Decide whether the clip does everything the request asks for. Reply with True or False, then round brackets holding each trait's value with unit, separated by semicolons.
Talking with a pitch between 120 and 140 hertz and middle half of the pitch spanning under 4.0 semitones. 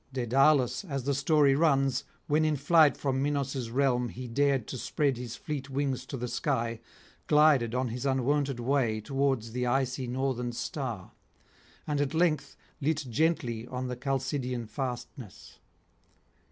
True (135 Hz; 2.6 semitones)